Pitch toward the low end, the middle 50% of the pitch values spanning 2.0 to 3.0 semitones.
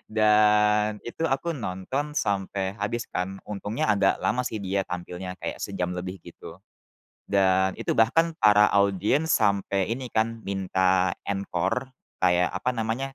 Yes: low, 100 Hz; narrow, 2.6 semitones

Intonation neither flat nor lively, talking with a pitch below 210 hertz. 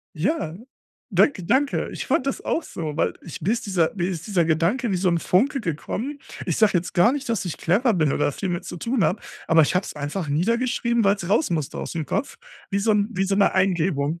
No: wide, 5.7 semitones; high, 190 Hz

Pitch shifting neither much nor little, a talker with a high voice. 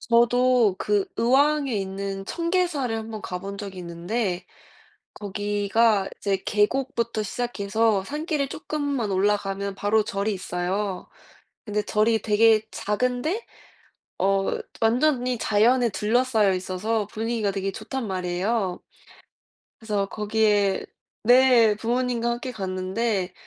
Yes: average, 3.6 semitones; high, 215 Hz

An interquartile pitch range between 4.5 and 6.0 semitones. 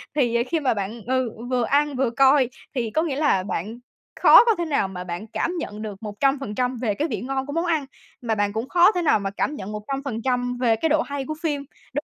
Yes: average, 4.9 semitones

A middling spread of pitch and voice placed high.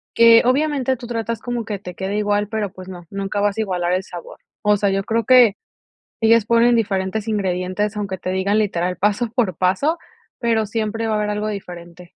Yes: average, 3.3 semitones; high, 210 Hz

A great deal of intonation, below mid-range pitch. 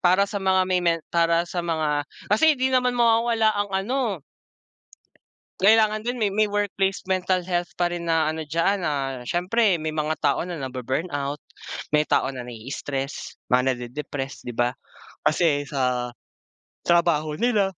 No: wide, 5.8 semitones; medium, 170 Hz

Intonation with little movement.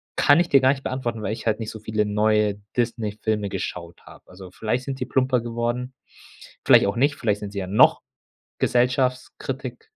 No: average, 3.5 semitones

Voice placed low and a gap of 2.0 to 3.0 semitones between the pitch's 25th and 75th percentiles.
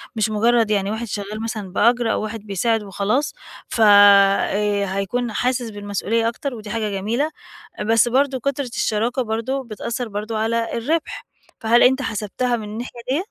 No: high, 225 Hz; average, 2.7 semitones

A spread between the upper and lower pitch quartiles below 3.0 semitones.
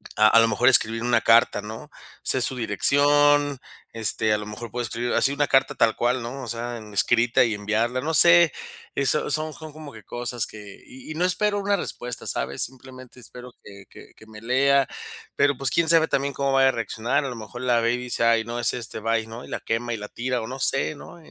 No: average, 3.4 semitones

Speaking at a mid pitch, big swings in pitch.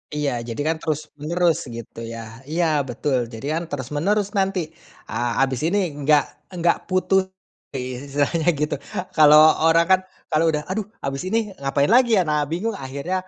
No: medium, 155 Hz; average, 4.6 semitones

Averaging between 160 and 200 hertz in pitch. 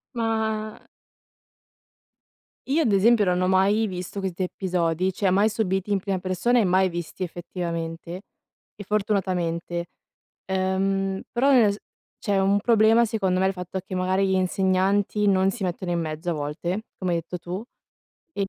Yes: high, 190 Hz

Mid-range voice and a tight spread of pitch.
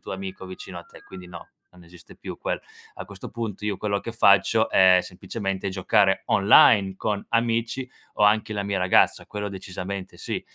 No: low, 100 Hz; narrow, 2.0 semitones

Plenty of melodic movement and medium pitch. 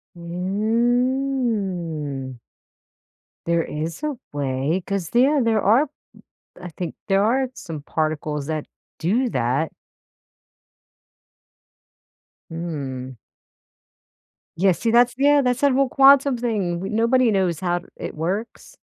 No: wide, 7.3 semitones; high, 195 Hz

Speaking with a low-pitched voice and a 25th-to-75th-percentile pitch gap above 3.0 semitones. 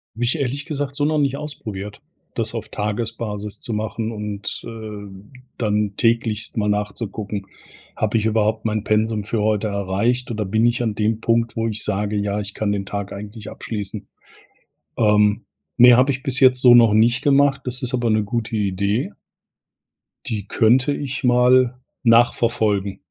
No: low, 110 Hz; average, 2.7 semitones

